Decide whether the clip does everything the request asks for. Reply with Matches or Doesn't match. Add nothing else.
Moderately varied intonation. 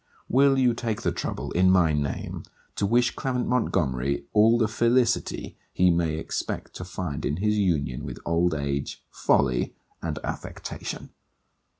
Doesn't match